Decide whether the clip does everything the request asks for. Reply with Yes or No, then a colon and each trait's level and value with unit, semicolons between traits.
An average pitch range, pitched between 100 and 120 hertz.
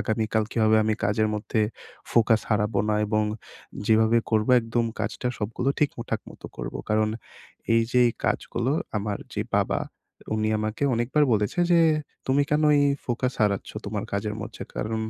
No: narrow, 1.8 semitones; low, 110 Hz